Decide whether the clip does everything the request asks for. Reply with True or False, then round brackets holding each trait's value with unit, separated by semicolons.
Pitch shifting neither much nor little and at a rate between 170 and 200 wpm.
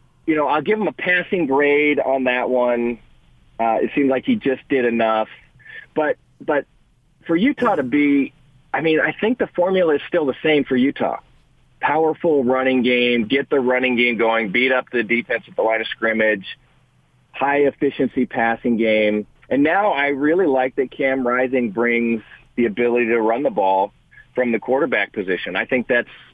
True (3.3 semitones; 180 wpm)